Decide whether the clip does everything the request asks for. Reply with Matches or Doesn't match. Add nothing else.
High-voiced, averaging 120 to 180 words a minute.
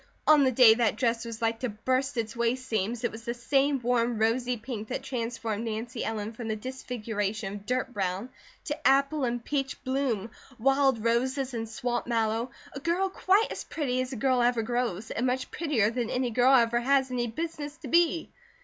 Doesn't match